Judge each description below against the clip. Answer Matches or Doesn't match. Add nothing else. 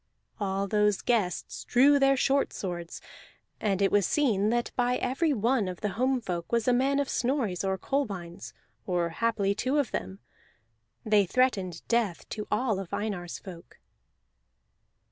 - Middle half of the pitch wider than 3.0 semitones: Matches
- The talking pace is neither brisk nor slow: Matches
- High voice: Matches